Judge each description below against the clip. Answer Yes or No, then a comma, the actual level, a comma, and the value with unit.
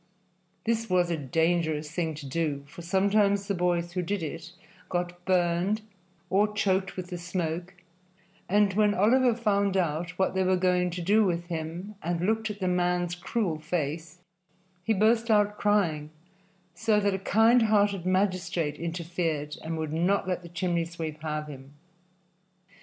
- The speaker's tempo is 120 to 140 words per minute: No, average, 160 wpm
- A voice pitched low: No, medium, 180 Hz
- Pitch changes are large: No, average, 3.3 semitones